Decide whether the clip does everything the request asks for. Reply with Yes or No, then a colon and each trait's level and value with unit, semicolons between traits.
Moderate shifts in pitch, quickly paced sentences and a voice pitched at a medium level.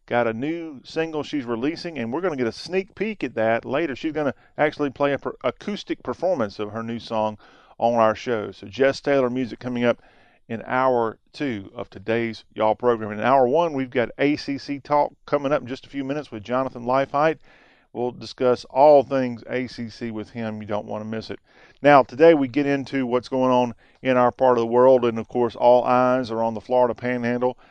No: average, 3.4 semitones; fast, 215 wpm; low, 125 Hz